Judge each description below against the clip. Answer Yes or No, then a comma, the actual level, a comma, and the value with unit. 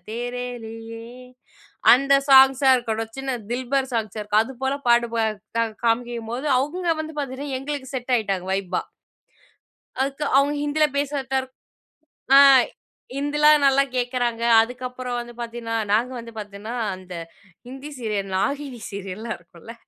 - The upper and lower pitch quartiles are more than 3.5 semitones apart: No, average, 3.1 semitones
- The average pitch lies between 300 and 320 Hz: No, high, 245 Hz